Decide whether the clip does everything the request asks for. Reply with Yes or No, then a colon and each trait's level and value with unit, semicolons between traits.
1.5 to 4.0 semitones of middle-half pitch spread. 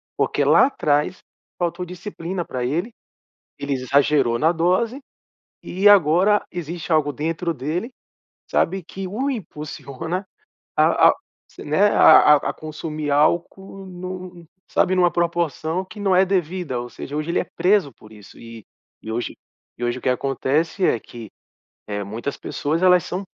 No: average, 4.5 semitones